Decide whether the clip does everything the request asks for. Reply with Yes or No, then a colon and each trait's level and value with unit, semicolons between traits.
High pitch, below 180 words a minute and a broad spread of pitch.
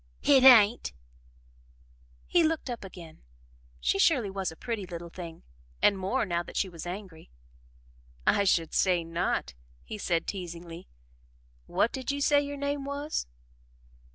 Yes: high, 195 Hz; average, 145 wpm; wide, 7.5 semitones